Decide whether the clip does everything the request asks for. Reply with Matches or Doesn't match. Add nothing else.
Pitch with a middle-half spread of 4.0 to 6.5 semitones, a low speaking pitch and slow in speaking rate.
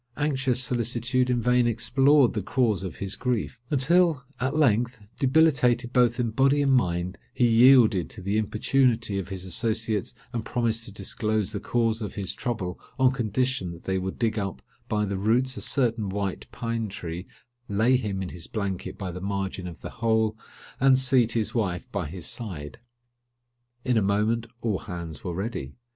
Doesn't match